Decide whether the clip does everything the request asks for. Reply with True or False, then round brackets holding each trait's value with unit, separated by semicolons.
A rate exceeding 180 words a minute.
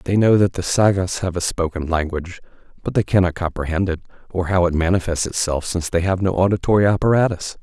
True (195 wpm)